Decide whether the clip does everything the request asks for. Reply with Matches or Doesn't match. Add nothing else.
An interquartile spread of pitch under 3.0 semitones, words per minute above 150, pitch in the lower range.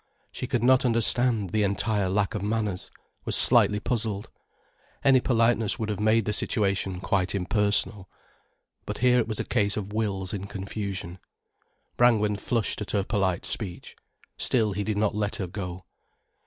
Matches